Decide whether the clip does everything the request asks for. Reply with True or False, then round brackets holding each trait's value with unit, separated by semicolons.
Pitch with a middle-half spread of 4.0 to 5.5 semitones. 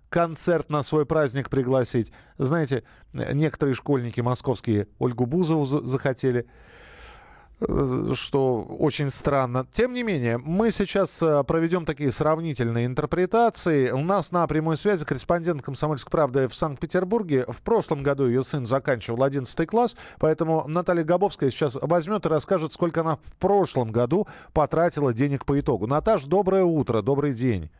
True (4.4 semitones)